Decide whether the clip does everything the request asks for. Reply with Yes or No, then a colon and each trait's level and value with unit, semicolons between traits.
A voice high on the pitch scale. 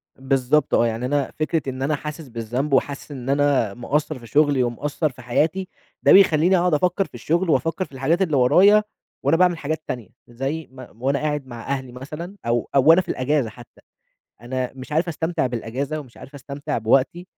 No: medium, 140 Hz